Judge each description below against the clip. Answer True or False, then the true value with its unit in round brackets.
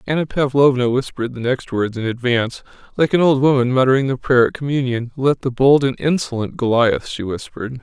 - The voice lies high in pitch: False (130 Hz)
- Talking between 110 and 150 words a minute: False (190 wpm)